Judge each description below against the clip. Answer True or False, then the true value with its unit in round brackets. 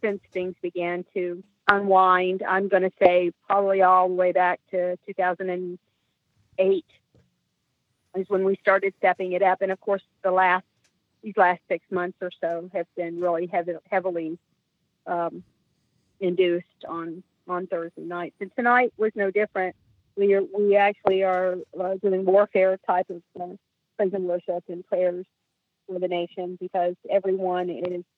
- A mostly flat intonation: True (1.4 semitones)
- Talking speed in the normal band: True (155 wpm)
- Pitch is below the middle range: False (185 Hz)